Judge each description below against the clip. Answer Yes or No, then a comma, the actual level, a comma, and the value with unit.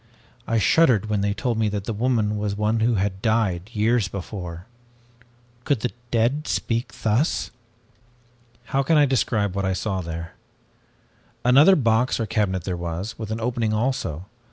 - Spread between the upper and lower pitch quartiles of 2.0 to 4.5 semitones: Yes, average, 3.5 semitones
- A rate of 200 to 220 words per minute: No, average, 160 wpm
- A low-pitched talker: Yes, low, 110 Hz